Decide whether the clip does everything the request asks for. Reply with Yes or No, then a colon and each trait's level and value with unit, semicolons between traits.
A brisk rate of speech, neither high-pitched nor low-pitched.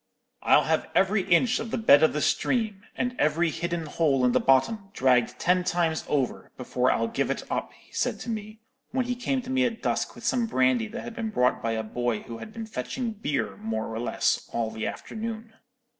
Yes: fast, 220 wpm; medium, 170 Hz